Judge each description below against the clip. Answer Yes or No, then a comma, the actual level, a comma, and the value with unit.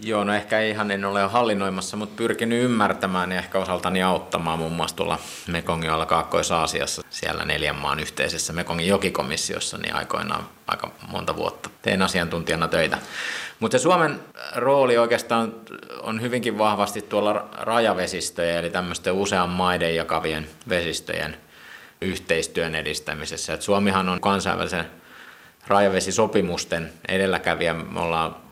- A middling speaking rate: Yes, average, 125 wpm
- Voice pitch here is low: Yes, very low, 95 Hz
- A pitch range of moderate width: Yes, average, 3.9 semitones